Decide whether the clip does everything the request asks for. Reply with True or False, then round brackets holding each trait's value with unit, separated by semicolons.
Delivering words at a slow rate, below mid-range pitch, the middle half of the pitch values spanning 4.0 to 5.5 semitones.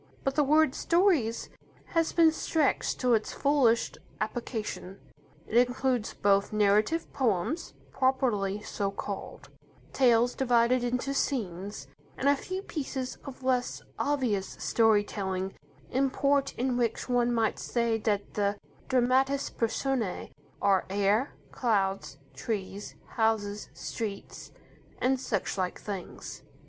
False (115 wpm; 235 Hz; 4.5 semitones)